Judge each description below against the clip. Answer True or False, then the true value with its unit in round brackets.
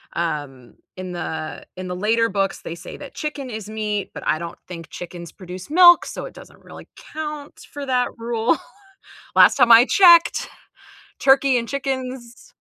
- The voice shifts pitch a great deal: True (7.2 semitones)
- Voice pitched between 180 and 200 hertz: False (230 Hz)